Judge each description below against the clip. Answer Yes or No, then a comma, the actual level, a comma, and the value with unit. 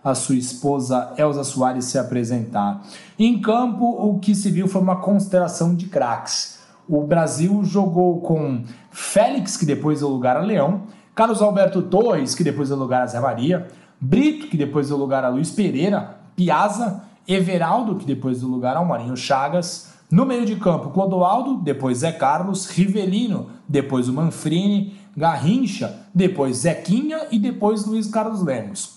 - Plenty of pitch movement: Yes, wide, 6.3 semitones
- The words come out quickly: No, average, 155 wpm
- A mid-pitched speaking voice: Yes, medium, 180 Hz